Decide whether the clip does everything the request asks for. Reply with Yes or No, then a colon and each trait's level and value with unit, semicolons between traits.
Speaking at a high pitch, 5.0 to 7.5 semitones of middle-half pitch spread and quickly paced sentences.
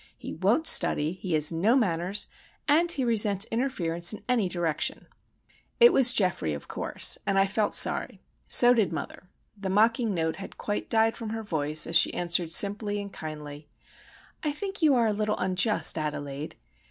No: high, 200 Hz; wide, 5.4 semitones; average, 170 wpm